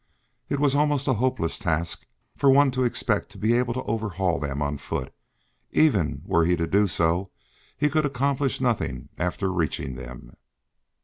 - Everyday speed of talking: Yes, average, 175 wpm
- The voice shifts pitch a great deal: Yes, wide, 7.9 semitones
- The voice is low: Yes, low, 105 Hz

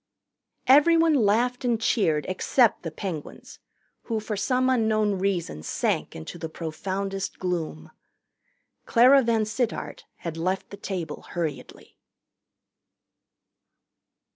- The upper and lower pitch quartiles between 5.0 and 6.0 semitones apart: Yes, wide, 5.4 semitones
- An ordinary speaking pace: No, slow, 100 wpm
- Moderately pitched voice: No, high, 200 Hz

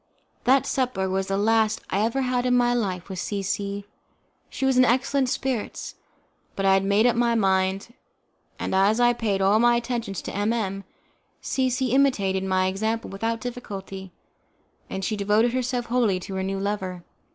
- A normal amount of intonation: Yes, average, 3.9 semitones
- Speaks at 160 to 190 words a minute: Yes, average, 180 wpm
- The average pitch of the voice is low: No, high, 215 Hz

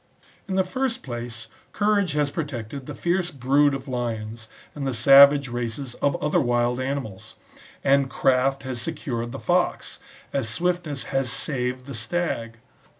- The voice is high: No, low, 135 Hz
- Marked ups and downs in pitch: No, average, 3.6 semitones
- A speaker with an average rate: Yes, average, 150 wpm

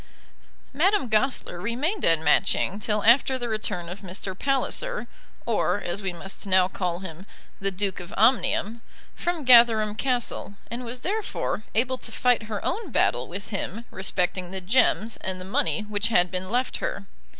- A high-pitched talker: Yes, high, 215 Hz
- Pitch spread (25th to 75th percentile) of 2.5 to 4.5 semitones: No, average, 4.9 semitones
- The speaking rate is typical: Yes, average, 165 wpm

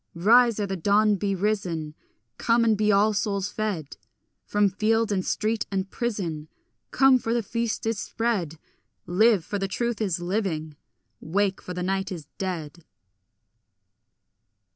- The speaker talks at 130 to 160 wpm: Yes, average, 140 wpm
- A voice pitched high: Yes, high, 200 Hz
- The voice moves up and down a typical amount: Yes, average, 3.3 semitones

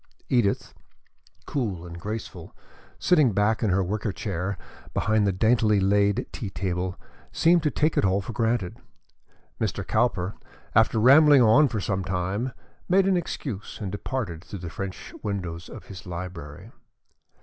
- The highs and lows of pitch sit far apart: No, average, 4.3 semitones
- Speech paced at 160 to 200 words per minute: No, average, 150 wpm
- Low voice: Yes, low, 100 Hz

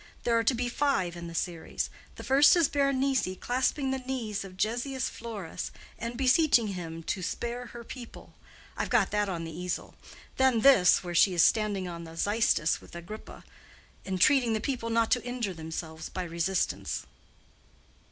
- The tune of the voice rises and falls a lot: Yes, wide, 6.0 semitones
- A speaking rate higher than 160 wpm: Yes, average, 170 wpm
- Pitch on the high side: Yes, high, 220 Hz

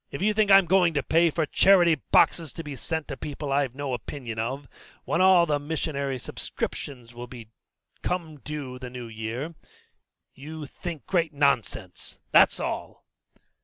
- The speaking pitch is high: No, medium, 145 Hz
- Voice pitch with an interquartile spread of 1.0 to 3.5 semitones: No, average, 4.5 semitones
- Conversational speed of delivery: Yes, average, 165 wpm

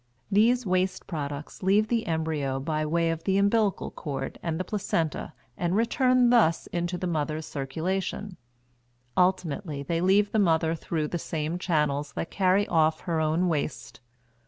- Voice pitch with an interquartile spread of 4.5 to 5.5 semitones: No, average, 3.8 semitones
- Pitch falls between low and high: Yes, medium, 170 Hz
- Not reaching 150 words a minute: No, average, 155 wpm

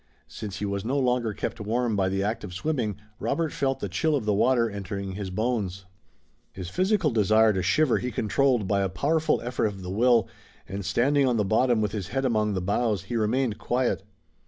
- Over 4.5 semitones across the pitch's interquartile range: No, average, 4.1 semitones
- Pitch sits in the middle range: No, low, 110 Hz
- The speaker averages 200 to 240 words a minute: Yes, fast, 205 wpm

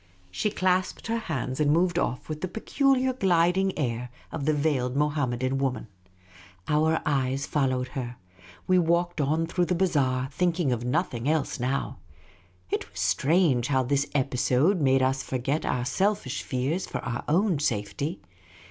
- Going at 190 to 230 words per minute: No, average, 155 wpm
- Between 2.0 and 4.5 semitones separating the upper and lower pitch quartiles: No, average, 5.2 semitones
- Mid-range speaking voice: Yes, medium, 145 Hz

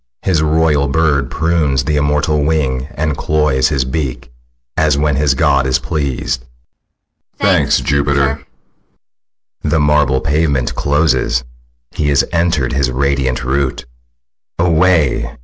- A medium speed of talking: No, slow, 125 wpm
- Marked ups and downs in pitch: No, narrow, 2.4 semitones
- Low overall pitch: Yes, very low, 70 Hz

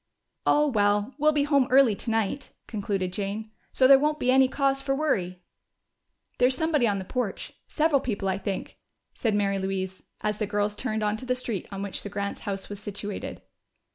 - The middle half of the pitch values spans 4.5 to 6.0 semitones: Yes, average, 4.9 semitones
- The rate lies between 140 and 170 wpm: No, average, 185 wpm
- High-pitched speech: Yes, high, 215 Hz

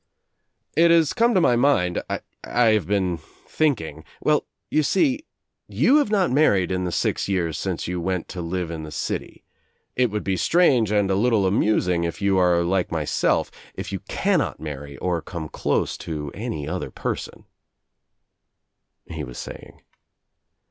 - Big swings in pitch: Yes, wide, 7.0 semitones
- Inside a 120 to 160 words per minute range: No, average, 170 wpm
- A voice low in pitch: Yes, very low, 95 Hz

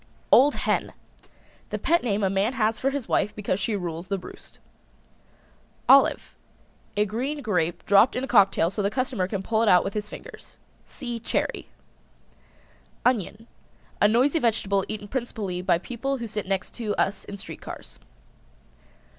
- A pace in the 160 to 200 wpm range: Yes, average, 165 wpm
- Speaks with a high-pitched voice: Yes, high, 210 Hz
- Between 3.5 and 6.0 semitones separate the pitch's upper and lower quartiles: Yes, average, 3.9 semitones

